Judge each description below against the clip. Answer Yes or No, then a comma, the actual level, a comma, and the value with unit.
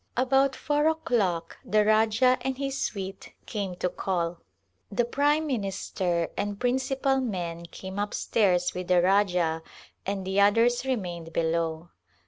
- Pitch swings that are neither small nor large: No, wide, 6.1 semitones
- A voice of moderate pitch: No, high, 200 Hz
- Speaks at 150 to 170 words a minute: No, average, 140 wpm